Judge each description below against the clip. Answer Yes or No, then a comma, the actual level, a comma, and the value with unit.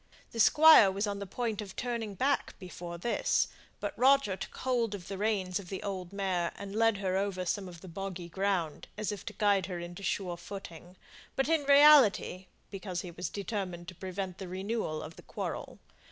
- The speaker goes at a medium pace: Yes, average, 195 wpm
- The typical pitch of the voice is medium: No, high, 195 Hz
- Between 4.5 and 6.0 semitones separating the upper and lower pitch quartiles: No, average, 2.9 semitones